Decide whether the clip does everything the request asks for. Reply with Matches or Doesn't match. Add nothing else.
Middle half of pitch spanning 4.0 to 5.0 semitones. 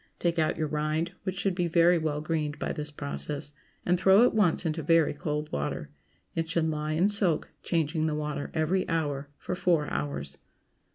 Doesn't match